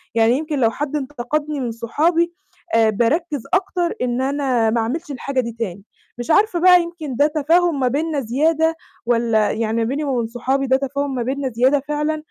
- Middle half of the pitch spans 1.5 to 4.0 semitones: No, average, 4.5 semitones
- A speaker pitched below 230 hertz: No, very high, 275 Hz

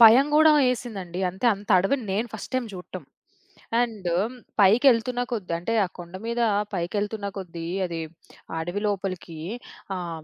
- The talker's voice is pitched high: Yes, high, 200 Hz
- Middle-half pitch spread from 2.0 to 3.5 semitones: No, average, 4.9 semitones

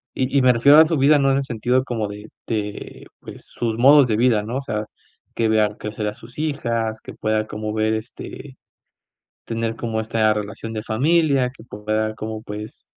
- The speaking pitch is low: Yes, low, 115 Hz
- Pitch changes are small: No, average, 3.1 semitones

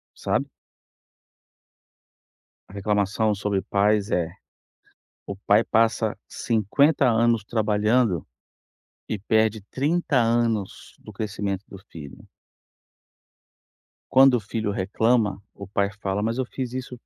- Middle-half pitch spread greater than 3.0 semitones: No, average, 2.7 semitones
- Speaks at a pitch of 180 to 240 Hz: No, low, 105 Hz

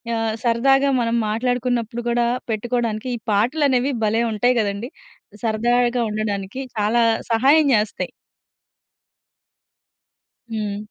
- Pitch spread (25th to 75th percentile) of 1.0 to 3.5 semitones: Yes, narrow, 2.4 semitones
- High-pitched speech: Yes, high, 235 Hz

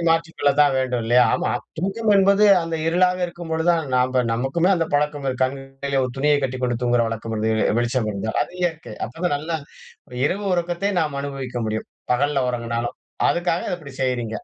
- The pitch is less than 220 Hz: Yes, medium, 140 Hz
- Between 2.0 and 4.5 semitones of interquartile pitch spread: No, average, 5.0 semitones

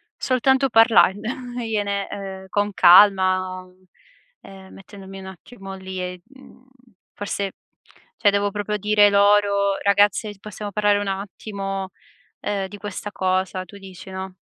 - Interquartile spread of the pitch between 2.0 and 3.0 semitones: No, narrow, 1.5 semitones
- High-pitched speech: Yes, high, 200 Hz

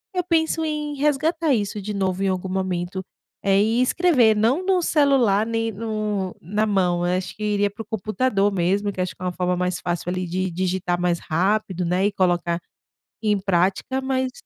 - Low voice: No, high, 200 Hz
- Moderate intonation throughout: Yes, average, 4.1 semitones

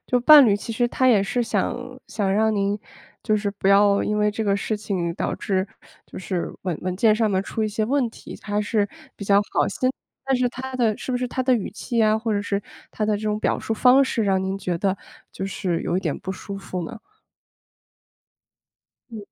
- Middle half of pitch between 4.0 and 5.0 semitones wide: No, average, 2.7 semitones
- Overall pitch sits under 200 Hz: No, high, 210 Hz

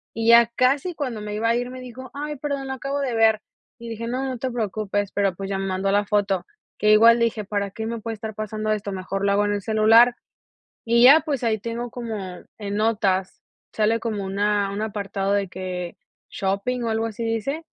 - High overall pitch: Yes, high, 220 Hz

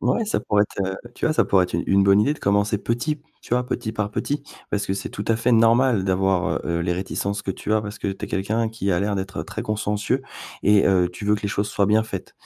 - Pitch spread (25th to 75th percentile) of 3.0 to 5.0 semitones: No, narrow, 2.5 semitones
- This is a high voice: No, low, 105 Hz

